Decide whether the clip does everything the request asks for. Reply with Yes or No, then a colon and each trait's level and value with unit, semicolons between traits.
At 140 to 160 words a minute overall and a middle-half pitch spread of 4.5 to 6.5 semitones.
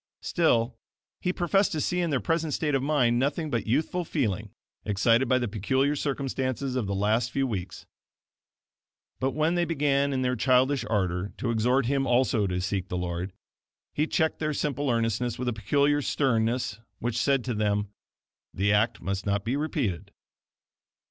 No: average, 170 wpm; average, 4.8 semitones